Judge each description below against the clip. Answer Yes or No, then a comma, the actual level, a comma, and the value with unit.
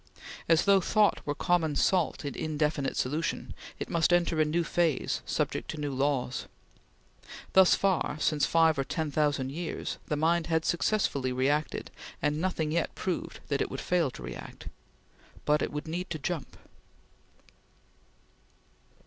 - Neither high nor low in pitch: Yes, medium, 155 Hz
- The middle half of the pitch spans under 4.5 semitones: Yes, average, 2.9 semitones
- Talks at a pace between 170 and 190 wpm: No, average, 150 wpm